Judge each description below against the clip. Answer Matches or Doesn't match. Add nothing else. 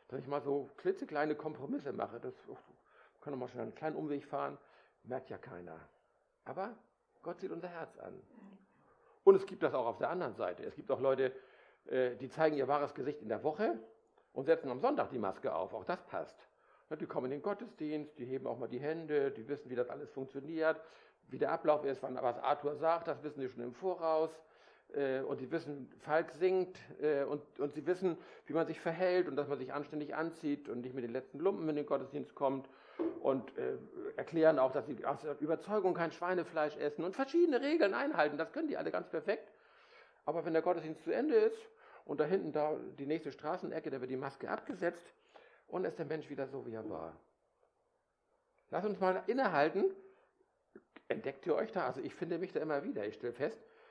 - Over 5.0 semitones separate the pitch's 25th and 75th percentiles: Matches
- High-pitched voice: Doesn't match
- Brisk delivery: Matches